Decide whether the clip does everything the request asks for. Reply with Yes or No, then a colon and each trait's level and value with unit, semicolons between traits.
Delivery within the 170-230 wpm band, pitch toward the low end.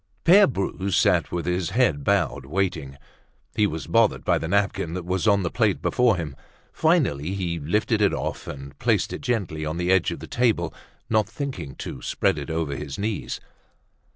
Yes: average, 185 wpm; very low, 90 Hz